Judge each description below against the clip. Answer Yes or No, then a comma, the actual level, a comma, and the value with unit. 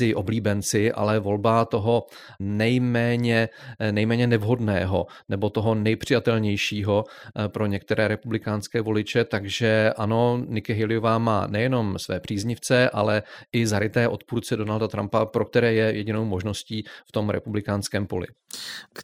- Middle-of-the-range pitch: No, low, 110 Hz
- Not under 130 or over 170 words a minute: No, slow, 115 wpm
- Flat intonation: Yes, narrow, 1.9 semitones